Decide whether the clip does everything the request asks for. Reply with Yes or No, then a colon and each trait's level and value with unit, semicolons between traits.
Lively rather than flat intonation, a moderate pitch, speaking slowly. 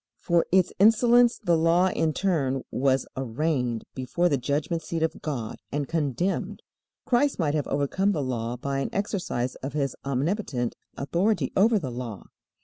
No: wide, 5.8 semitones; medium, 150 Hz; average, 155 wpm